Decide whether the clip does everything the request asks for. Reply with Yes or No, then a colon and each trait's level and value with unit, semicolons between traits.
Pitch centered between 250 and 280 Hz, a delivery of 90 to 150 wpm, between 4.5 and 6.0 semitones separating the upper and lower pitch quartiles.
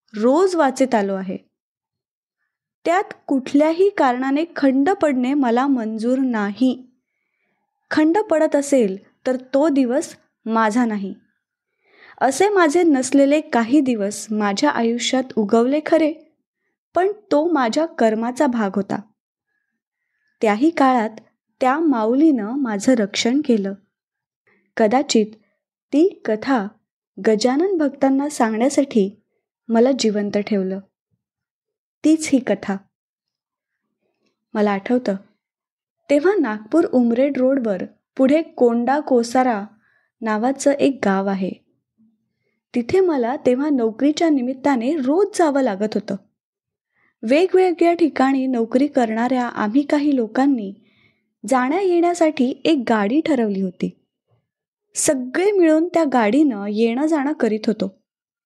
Yes: very high, 260 Hz; average, 100 wpm; wide, 5.6 semitones